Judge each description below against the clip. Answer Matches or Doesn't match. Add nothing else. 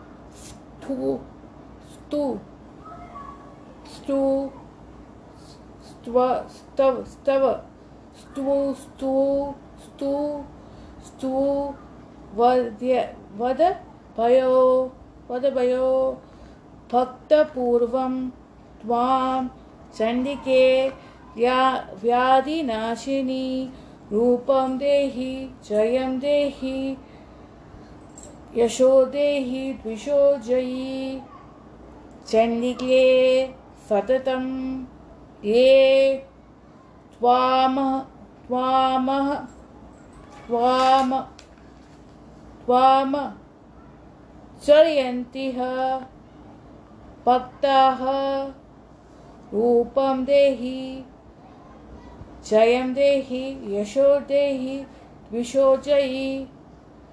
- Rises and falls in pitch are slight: Matches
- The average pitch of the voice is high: Matches